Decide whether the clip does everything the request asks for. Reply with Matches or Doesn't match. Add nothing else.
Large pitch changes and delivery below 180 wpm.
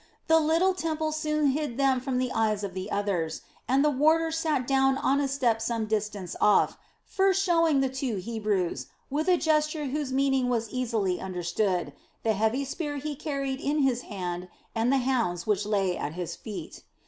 Doesn't match